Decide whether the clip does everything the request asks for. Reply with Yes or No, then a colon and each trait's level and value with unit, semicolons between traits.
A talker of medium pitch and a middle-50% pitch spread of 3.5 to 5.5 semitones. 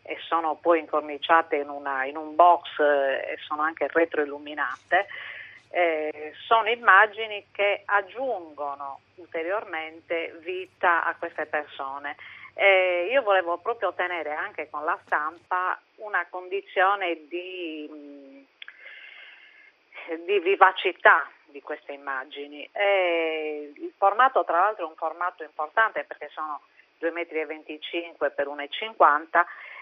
Yes: medium, 165 Hz; average, 4.2 semitones